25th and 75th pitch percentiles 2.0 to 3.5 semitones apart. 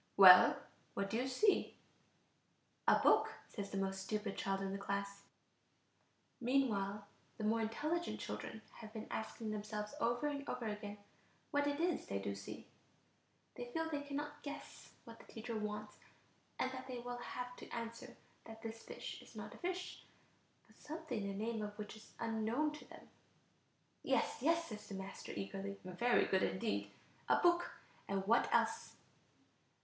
No: average, 4.7 semitones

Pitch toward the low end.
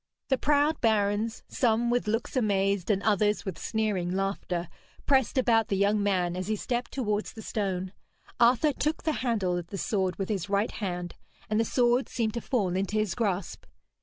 No: high, 210 Hz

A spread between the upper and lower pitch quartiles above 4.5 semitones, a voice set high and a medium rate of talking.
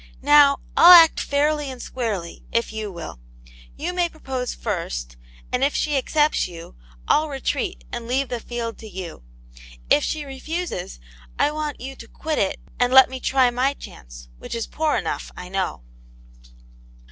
Yes: wide, 5.6 semitones; very high, 260 Hz; average, 165 wpm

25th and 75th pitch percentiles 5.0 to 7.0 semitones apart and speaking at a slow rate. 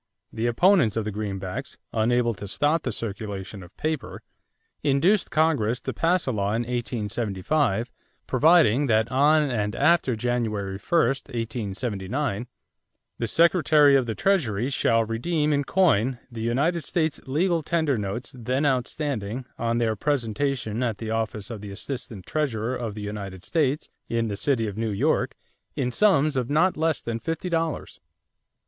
No: wide, 5.4 semitones; average, 155 wpm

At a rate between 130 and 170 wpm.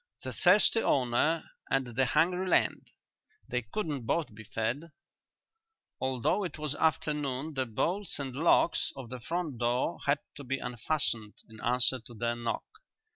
Yes: average, 150 wpm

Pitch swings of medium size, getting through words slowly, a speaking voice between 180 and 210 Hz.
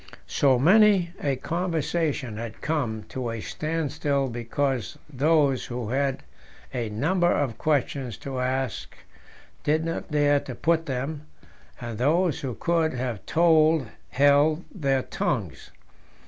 No: average, 4.1 semitones; slow, 125 wpm; medium, 140 Hz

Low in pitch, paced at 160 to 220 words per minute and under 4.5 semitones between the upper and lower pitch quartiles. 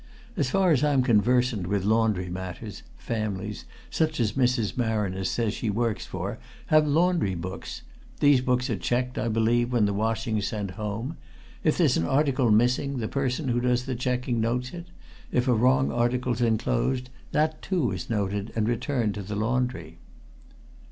Yes: low, 120 Hz; average, 165 wpm; average, 3.2 semitones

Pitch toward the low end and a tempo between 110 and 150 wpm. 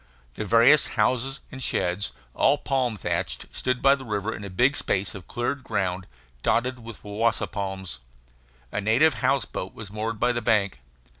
No: low, 115 Hz; average, 170 wpm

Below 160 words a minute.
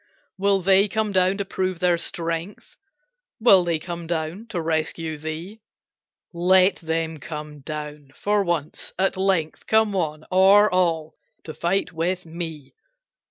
Yes: average, 140 wpm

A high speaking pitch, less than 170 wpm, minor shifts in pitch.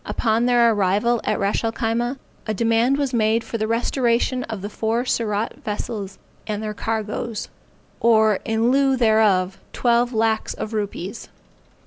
Yes: high, 225 Hz; average, 150 wpm; narrow, 1.9 semitones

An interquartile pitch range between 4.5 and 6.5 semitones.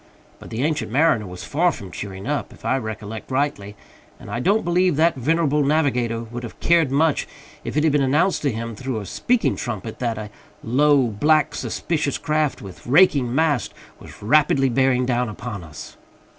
Yes: average, 5.1 semitones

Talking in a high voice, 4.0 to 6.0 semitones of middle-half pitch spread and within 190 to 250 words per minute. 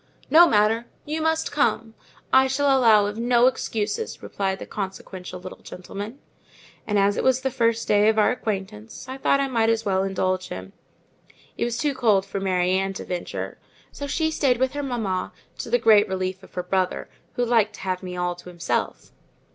Yes: high, 215 Hz; average, 4.7 semitones; average, 195 wpm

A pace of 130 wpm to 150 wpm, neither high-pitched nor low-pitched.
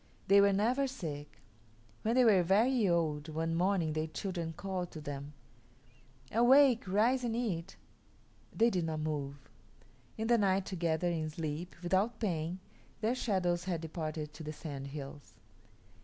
Yes: average, 145 wpm; medium, 175 Hz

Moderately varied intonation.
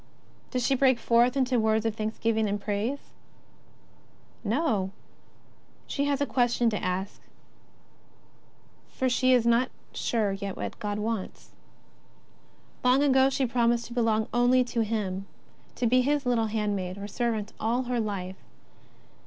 Yes: average, 3.1 semitones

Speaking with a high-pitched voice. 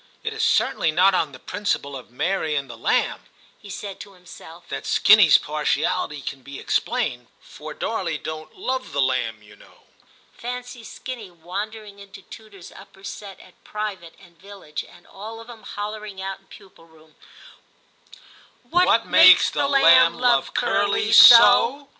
Yes: high, 195 Hz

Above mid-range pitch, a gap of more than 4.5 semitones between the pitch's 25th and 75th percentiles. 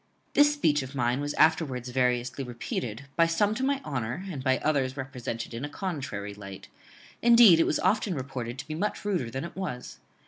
No: low, 135 Hz; wide, 5.6 semitones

